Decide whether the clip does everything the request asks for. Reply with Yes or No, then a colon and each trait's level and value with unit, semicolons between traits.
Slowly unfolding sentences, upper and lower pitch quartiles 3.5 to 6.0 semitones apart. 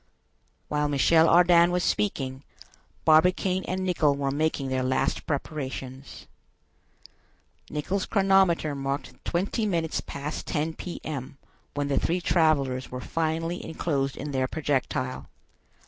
Yes: slow, 115 wpm; average, 4.0 semitones